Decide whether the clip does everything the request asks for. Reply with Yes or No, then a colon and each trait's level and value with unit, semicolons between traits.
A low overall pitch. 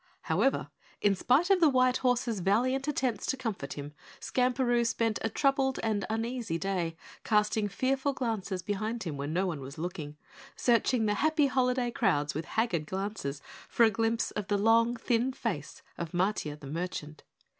No: high, 220 Hz